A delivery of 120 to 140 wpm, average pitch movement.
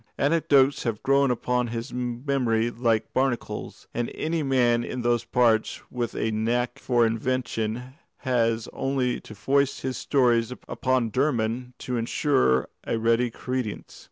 No: slow, 135 wpm; narrow, 2.2 semitones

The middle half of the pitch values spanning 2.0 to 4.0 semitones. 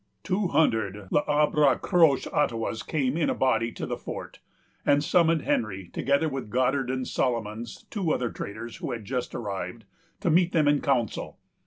No: average, 5.0 semitones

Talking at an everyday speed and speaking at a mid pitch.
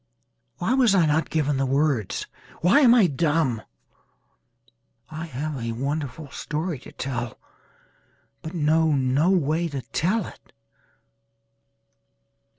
No: slow, 115 wpm; medium, 155 Hz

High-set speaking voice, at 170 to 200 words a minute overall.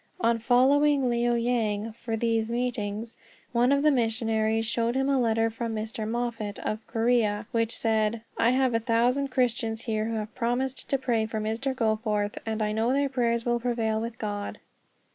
Yes: high, 230 Hz; average, 180 wpm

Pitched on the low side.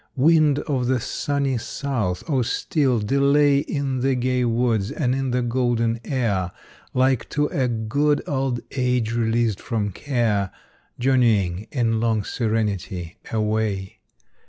Yes: low, 120 Hz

